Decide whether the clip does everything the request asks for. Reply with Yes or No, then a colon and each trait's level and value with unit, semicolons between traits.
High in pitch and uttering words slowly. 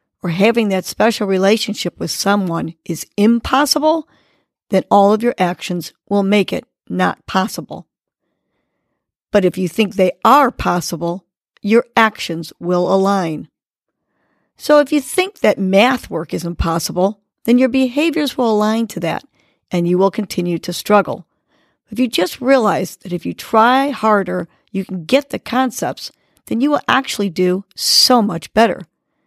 No: high, 205 Hz; average, 150 wpm